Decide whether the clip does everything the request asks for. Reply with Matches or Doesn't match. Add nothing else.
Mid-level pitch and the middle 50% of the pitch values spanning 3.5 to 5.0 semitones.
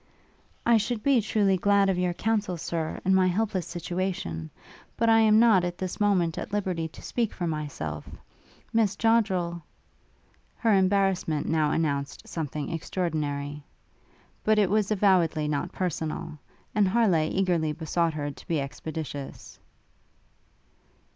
Matches